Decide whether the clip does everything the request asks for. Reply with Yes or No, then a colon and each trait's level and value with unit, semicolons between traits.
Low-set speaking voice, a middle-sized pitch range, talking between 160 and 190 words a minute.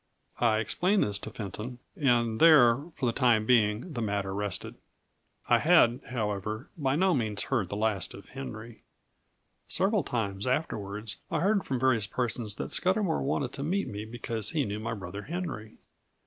Yes: low, 115 Hz; average, 4.7 semitones; average, 165 wpm